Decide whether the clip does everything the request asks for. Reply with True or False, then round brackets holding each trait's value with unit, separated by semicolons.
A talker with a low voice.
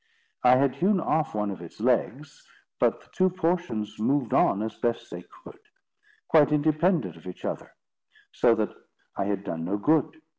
True (125 Hz)